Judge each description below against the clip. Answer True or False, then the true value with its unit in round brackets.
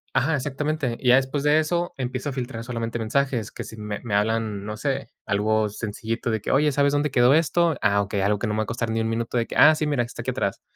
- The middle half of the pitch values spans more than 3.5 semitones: True (4.5 semitones)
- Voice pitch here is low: True (120 Hz)